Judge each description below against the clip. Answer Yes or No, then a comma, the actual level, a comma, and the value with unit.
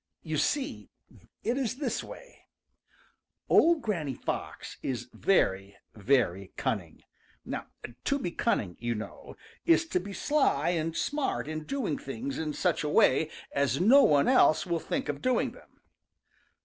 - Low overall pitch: No, medium, 160 Hz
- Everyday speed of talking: Yes, average, 145 wpm